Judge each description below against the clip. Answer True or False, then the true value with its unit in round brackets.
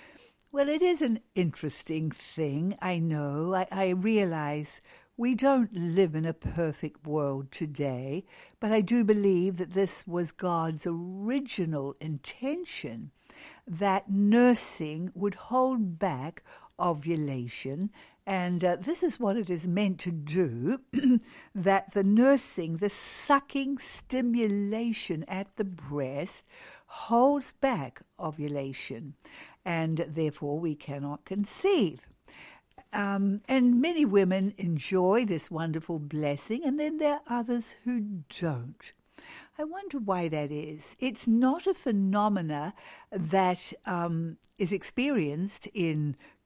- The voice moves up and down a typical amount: False (6.6 semitones)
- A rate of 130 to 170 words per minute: False (120 wpm)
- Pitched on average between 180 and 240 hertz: True (190 Hz)